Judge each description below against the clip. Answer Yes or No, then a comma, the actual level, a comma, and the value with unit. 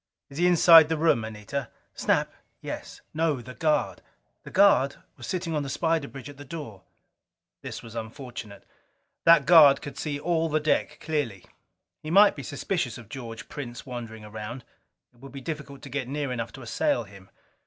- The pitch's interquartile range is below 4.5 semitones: No, average, 5.0 semitones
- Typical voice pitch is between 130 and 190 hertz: Yes, medium, 140 Hz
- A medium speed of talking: Yes, average, 180 wpm